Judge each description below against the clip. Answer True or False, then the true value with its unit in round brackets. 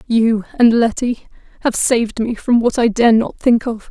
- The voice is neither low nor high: False (230 Hz)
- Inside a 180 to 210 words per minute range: True (200 wpm)